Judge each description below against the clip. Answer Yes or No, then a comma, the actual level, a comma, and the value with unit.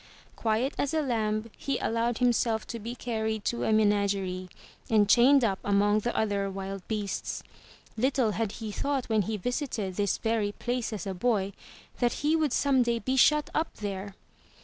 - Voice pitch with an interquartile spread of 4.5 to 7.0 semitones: No, average, 3.2 semitones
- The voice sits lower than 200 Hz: No, high, 220 Hz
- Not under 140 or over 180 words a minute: Yes, average, 175 wpm